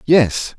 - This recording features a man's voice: Yes, male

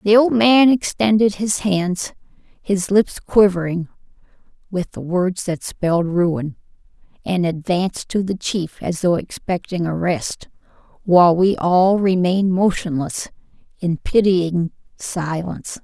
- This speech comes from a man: No, female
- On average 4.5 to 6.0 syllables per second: No, 4.0 syllables/s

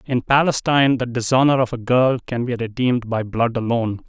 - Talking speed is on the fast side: No, average, 190 wpm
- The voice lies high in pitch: No, low, 120 Hz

